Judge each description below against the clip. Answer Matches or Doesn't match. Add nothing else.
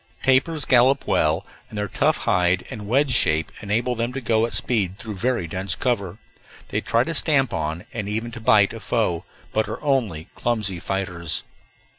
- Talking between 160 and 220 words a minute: Matches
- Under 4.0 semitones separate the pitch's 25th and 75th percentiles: Doesn't match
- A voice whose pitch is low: Matches